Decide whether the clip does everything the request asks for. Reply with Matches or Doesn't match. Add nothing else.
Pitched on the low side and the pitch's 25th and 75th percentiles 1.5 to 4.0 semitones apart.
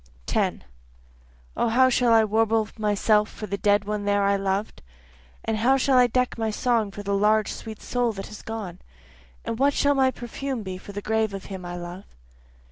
Doesn't match